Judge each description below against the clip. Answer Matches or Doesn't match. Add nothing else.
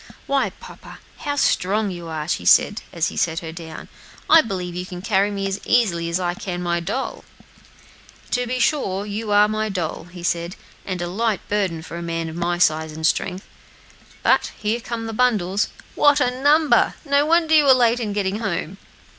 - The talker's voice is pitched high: Matches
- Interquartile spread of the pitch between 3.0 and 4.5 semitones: Doesn't match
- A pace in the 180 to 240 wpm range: Matches